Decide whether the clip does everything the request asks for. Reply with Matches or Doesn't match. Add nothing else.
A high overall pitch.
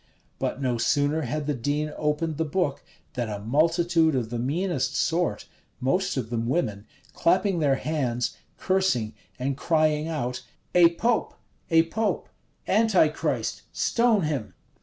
Doesn't match